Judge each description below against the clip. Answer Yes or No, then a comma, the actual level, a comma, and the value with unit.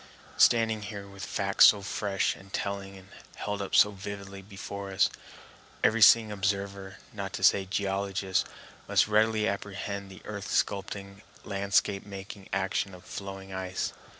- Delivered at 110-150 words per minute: Yes, average, 145 wpm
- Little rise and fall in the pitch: Yes, narrow, 0.9 semitones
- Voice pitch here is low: Yes, low, 100 Hz